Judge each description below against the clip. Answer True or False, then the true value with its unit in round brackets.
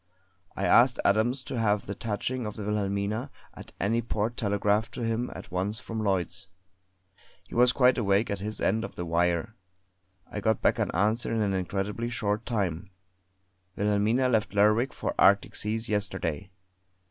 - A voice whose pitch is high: False (105 Hz)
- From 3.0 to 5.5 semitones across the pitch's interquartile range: False (2.4 semitones)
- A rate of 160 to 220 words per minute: True (165 wpm)